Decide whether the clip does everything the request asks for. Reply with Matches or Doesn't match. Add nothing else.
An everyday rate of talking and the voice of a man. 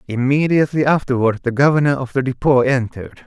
Matches